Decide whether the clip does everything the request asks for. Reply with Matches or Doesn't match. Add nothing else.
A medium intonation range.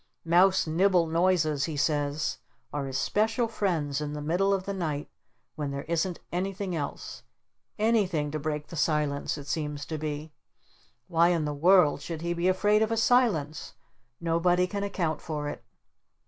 Matches